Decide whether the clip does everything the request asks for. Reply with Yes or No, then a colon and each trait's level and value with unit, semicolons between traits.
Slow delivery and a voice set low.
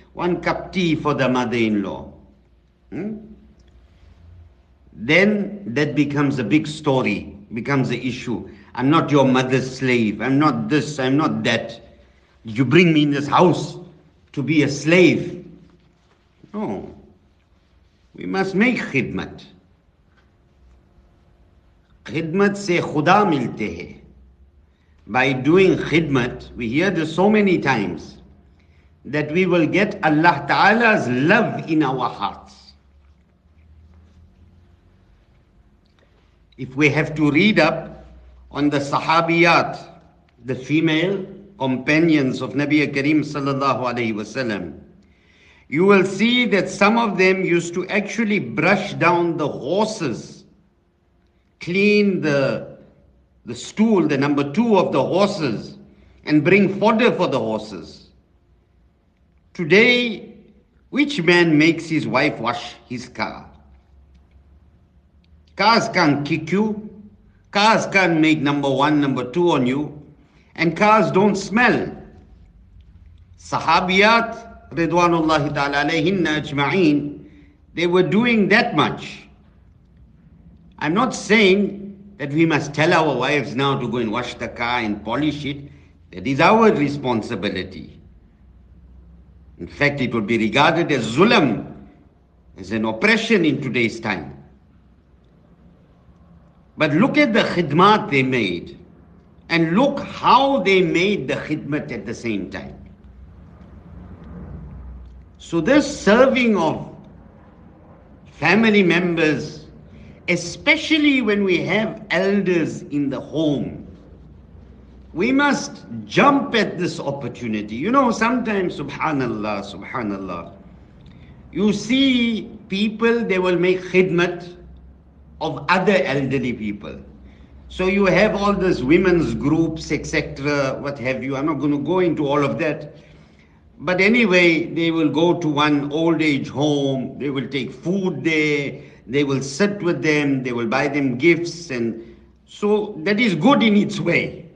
No: slow, 120 wpm; medium, 145 Hz